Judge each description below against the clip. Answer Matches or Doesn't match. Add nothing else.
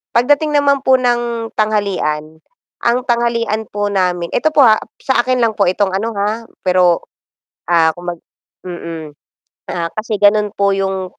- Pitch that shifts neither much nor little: Matches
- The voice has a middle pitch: Doesn't match